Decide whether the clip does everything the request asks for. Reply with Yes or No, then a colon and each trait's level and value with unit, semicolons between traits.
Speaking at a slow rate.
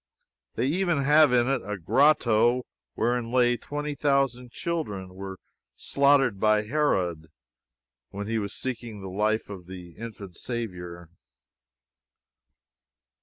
Yes: slow, 115 wpm